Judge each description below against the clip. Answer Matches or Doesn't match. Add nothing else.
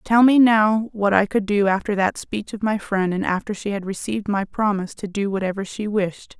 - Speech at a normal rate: Doesn't match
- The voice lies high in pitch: Matches